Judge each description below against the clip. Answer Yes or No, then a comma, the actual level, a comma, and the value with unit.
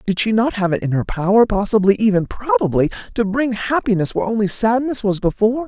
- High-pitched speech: Yes, high, 215 Hz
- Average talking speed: Yes, average, 180 wpm